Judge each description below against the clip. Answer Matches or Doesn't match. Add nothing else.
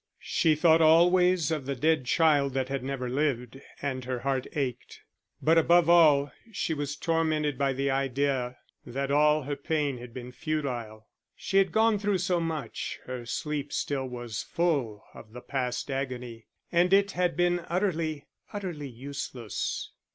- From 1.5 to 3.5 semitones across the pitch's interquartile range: Doesn't match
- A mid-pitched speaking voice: Matches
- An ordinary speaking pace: Matches